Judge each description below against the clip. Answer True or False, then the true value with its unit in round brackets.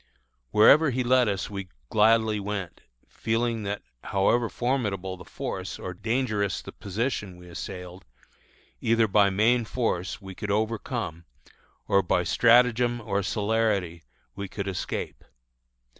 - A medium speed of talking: False (130 wpm)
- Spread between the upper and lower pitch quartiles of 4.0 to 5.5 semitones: False (3.2 semitones)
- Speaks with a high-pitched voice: False (105 Hz)